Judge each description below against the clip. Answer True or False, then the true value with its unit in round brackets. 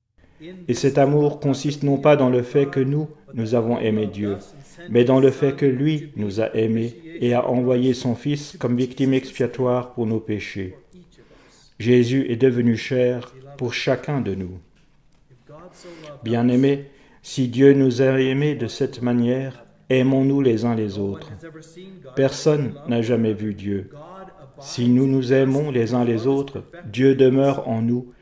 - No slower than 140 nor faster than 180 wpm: True (155 wpm)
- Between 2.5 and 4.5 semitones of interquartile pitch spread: True (2.9 semitones)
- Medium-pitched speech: False (130 Hz)